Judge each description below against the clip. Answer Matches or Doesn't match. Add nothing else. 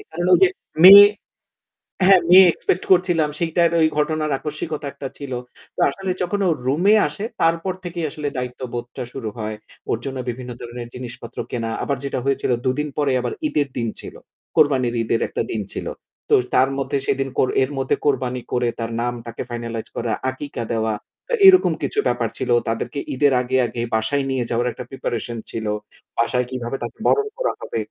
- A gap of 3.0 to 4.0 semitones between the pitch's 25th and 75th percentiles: Doesn't match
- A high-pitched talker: Doesn't match